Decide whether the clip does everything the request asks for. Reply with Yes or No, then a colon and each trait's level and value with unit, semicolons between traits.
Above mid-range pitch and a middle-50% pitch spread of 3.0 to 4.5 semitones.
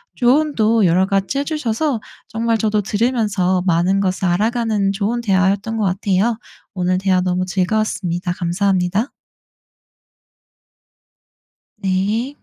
Yes: high, 200 Hz; average, 3.4 semitones